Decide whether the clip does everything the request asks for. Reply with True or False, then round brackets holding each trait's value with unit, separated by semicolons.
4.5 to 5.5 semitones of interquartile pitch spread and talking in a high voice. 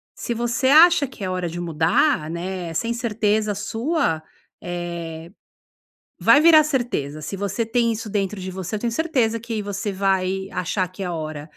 True (5.1 semitones; 200 Hz)